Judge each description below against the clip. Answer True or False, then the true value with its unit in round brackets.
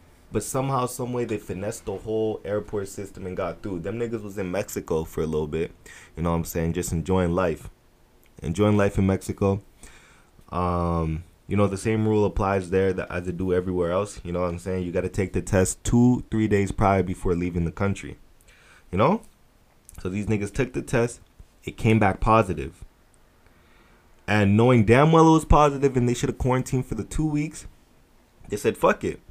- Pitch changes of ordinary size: True (3.9 semitones)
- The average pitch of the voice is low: True (100 Hz)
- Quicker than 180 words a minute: True (200 wpm)